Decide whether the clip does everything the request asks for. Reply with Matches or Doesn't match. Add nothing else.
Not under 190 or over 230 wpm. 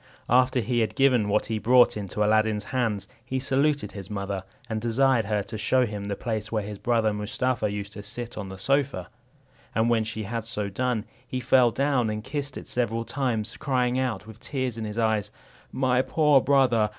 Matches